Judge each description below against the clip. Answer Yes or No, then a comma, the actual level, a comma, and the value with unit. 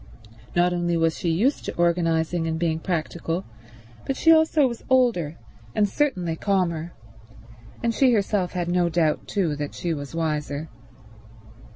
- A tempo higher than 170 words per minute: No, average, 150 wpm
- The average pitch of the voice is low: No, medium, 175 Hz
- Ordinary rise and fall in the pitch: Yes, average, 3.8 semitones